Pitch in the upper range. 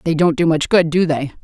No: medium, 160 Hz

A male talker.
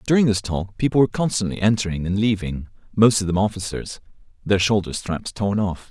Yes: male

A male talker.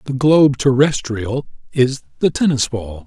Yes: male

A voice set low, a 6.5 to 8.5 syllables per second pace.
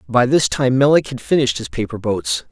No: low, 125 Hz; 5.6 syllables/s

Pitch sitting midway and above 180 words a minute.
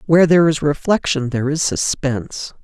No: medium, 145 Hz; average, 160 wpm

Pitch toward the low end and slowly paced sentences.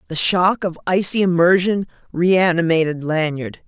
No: medium, 175 Hz; slow, 115 wpm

